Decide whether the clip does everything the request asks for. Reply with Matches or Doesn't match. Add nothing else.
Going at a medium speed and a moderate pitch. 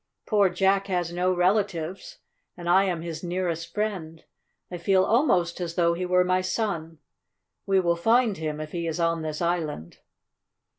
Matches